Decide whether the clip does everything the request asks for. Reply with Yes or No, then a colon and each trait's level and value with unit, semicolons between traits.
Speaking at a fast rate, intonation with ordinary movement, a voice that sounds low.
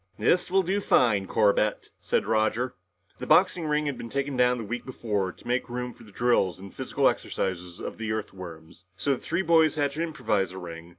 No: fast, 210 wpm; wide, 6.3 semitones; low, 115 Hz